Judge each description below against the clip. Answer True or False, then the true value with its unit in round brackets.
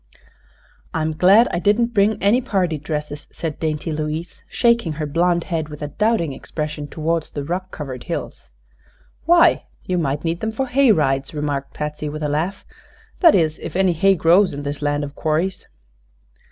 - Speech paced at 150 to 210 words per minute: True (175 wpm)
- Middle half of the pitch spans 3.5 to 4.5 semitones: True (4.2 semitones)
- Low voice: False (160 Hz)